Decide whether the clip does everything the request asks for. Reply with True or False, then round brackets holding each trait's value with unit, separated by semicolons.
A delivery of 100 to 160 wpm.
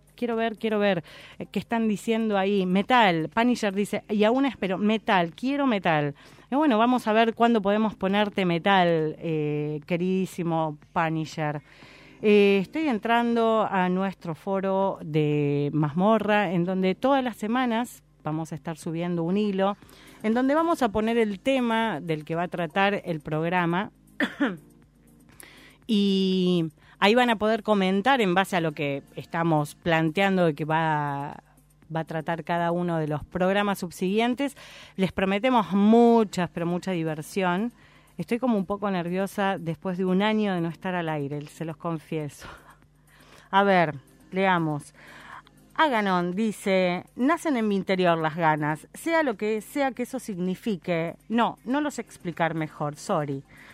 True (150 wpm)